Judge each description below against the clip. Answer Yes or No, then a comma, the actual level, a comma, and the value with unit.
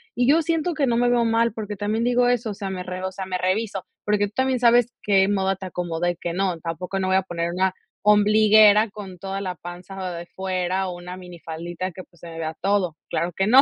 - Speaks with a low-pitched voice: No, high, 190 Hz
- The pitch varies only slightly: No, average, 3.2 semitones